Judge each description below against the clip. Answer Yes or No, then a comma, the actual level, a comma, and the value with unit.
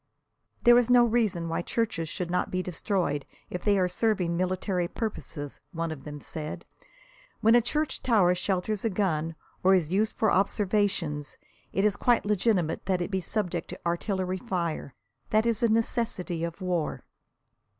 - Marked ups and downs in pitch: No, average, 4.1 semitones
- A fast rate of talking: No, average, 165 wpm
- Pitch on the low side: No, medium, 185 Hz